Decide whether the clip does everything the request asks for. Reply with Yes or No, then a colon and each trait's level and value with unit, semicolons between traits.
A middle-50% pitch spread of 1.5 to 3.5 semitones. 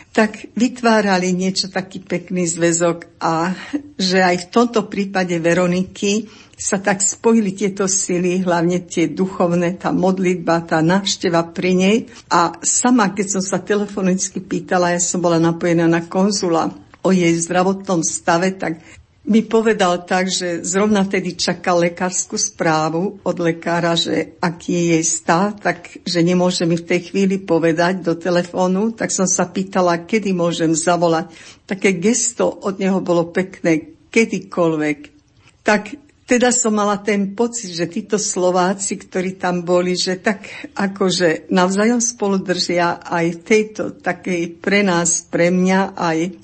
Yes: average, 2.7 semitones